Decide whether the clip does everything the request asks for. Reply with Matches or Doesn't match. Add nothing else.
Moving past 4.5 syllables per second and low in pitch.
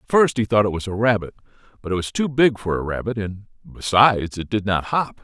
Matches